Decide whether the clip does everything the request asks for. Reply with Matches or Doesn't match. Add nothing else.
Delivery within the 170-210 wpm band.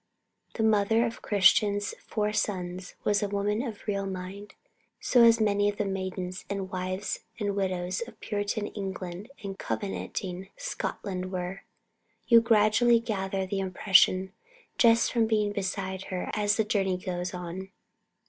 Doesn't match